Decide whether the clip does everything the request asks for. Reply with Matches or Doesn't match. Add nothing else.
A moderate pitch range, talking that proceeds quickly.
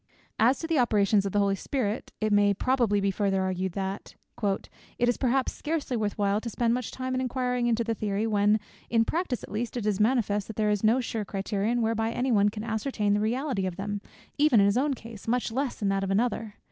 Matches